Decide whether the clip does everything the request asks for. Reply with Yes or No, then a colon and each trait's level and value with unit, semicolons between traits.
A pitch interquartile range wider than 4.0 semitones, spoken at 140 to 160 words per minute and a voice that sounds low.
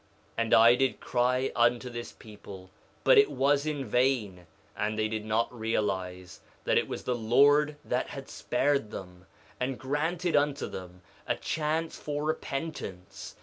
Yes: average, 5.1 semitones; average, 155 wpm; low, 125 Hz